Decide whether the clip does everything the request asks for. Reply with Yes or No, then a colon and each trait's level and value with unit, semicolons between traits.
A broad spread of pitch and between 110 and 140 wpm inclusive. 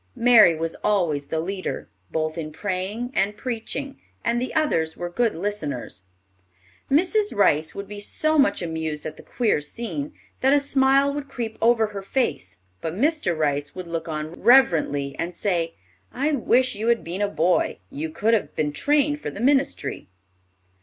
No: wide, 8.2 semitones; average, 170 wpm